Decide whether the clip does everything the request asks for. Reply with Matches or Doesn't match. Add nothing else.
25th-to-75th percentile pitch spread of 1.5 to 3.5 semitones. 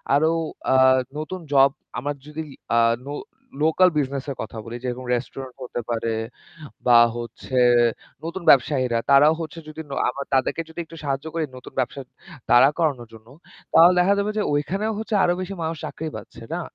Doesn't match